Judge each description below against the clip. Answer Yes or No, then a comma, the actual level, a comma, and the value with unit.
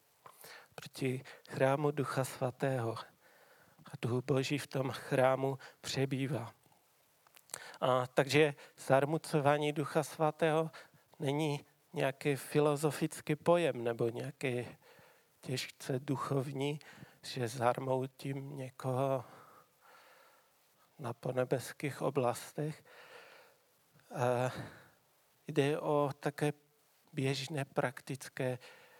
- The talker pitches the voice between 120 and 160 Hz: Yes, medium, 140 Hz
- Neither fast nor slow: No, slow, 75 wpm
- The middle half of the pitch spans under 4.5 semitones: Yes, average, 2.7 semitones